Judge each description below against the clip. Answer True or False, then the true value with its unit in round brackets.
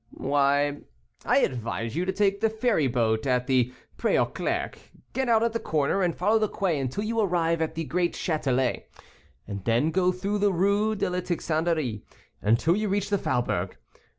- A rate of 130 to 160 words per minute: False (185 wpm)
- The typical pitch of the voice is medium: True (170 Hz)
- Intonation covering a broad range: True (7.3 semitones)